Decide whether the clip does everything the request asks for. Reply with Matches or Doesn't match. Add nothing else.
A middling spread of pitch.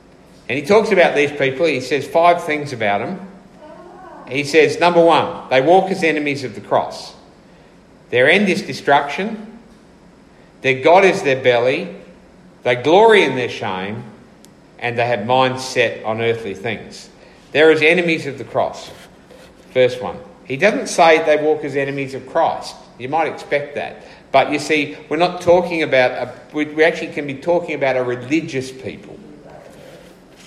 Matches